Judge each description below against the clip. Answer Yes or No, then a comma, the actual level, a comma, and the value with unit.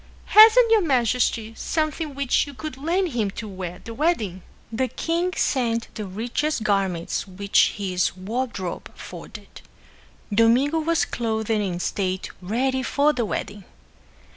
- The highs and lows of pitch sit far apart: Yes, wide, 6.7 semitones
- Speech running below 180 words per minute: Yes, average, 140 wpm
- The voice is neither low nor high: No, high, 230 Hz